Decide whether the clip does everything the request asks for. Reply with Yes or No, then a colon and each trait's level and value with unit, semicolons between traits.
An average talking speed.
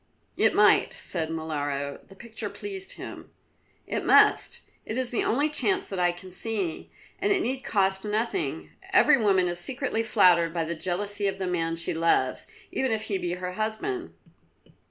Yes: average, 175 wpm